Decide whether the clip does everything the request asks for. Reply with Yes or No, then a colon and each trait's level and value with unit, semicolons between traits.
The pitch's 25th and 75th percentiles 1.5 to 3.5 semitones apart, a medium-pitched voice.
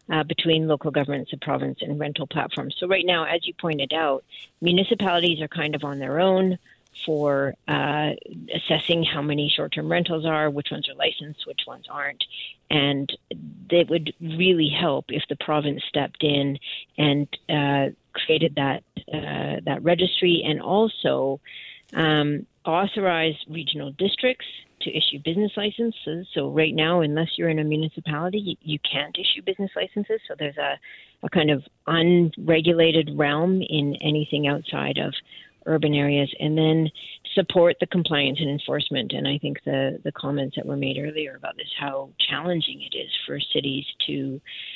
Yes: average, 2.9 semitones; medium, 155 Hz